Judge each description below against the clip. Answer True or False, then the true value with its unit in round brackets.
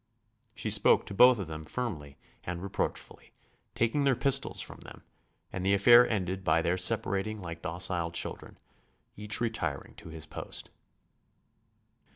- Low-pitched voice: True (95 Hz)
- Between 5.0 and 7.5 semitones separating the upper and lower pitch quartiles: True (5.3 semitones)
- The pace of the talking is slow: False (145 wpm)